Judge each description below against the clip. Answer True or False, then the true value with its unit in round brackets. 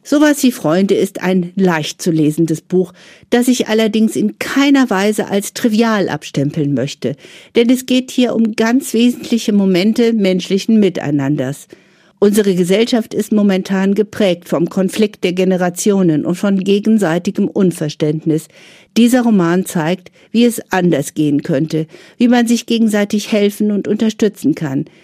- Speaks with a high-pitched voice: True (200 Hz)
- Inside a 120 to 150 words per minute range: True (140 wpm)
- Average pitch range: True (4.4 semitones)